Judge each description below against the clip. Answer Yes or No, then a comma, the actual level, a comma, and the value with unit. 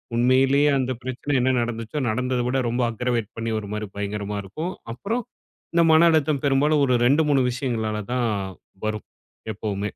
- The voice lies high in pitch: No, low, 125 Hz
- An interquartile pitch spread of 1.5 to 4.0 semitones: No, average, 4.4 semitones